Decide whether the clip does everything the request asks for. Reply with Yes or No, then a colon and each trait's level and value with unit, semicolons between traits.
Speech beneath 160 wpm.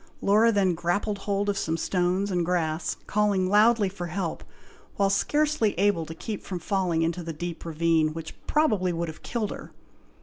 No: average, 175 wpm